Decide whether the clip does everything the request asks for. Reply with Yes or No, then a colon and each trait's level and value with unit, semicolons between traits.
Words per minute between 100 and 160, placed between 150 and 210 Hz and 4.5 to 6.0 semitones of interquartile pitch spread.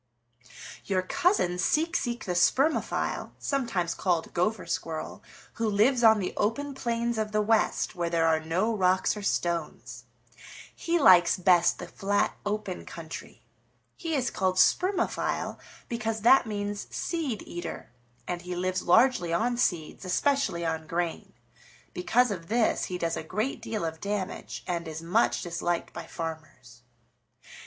Yes: average, 145 wpm; high, 190 Hz; average, 5.2 semitones